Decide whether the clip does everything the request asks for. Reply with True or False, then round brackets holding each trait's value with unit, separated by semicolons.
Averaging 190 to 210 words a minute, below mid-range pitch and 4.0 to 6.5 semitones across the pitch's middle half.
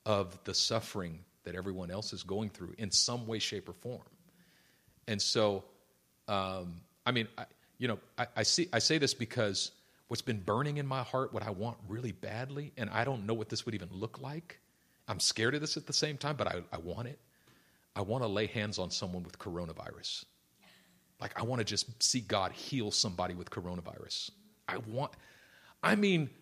True (200 wpm; 110 Hz; 4.8 semitones)